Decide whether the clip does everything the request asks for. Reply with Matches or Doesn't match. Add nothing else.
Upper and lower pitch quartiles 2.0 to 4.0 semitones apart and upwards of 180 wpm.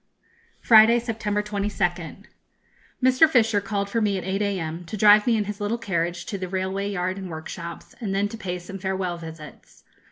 Matches